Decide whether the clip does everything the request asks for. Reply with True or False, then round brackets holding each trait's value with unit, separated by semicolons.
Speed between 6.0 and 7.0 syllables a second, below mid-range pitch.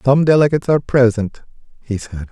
True (6.2 syllables/s; 130 Hz)